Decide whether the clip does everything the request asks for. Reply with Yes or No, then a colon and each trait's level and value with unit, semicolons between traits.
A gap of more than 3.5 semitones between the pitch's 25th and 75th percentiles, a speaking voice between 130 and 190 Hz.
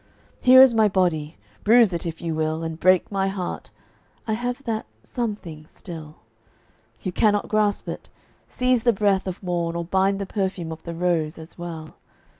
Yes: average, 4.3 semitones; medium, 185 Hz